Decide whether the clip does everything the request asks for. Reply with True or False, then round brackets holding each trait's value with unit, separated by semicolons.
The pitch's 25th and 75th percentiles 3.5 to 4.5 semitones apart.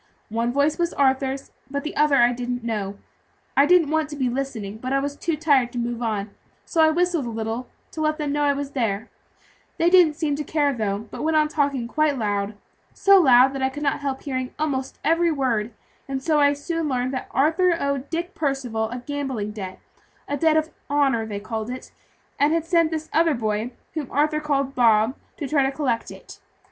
True (4.2 semitones)